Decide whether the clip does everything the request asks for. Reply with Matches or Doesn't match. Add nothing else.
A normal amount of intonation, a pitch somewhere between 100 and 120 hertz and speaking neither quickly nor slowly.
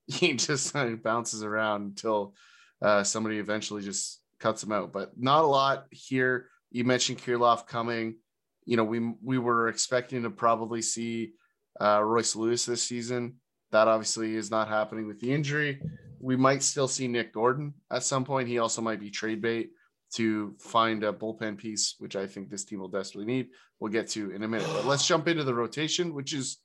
Matches